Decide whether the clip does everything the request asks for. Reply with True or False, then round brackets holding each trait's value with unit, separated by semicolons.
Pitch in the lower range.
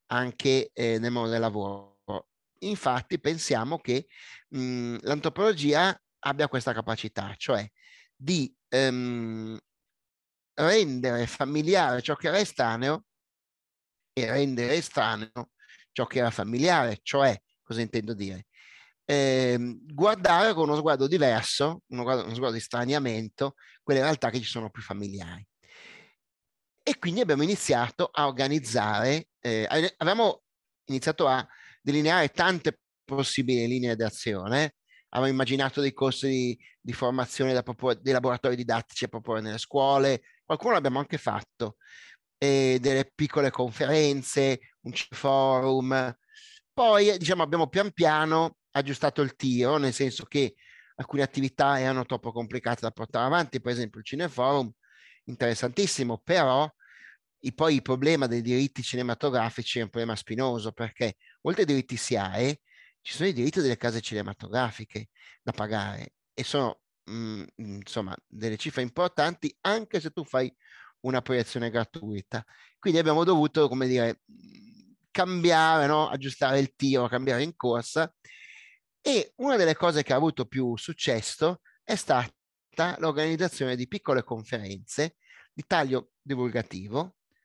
True (130 Hz)